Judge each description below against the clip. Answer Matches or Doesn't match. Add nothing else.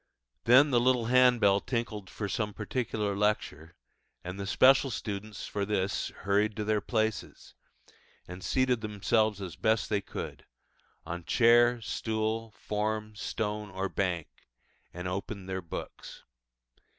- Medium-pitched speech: Doesn't match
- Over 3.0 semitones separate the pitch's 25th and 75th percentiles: Doesn't match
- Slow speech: Matches